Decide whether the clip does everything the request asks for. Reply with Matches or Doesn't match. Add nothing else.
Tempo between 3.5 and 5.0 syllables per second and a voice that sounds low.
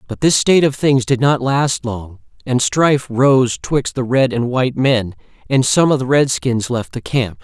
Matches